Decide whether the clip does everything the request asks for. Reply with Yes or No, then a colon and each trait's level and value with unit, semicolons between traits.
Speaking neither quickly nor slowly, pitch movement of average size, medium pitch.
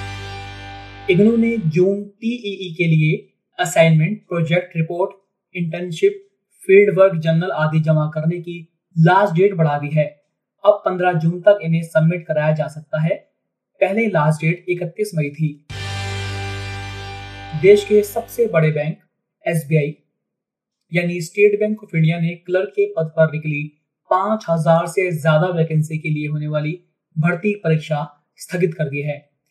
Yes: average, 140 wpm; average, 3.9 semitones; medium, 165 Hz